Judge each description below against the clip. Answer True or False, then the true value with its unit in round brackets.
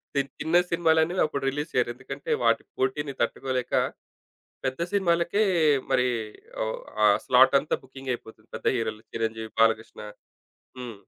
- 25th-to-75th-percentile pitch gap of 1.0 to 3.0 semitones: False (5.6 semitones)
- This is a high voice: False (130 Hz)